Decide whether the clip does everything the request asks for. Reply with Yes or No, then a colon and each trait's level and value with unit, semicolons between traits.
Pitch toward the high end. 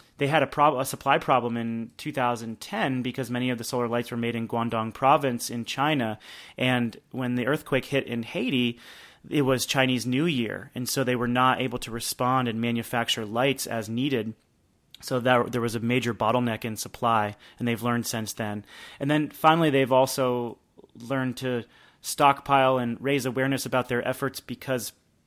No: low, 125 Hz